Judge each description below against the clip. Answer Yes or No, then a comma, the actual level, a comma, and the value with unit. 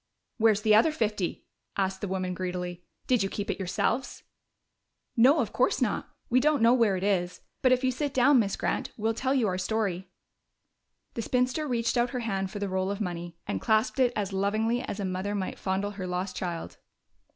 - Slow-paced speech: No, fast, 205 wpm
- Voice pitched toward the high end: Yes, high, 205 Hz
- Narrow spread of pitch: No, average, 4.3 semitones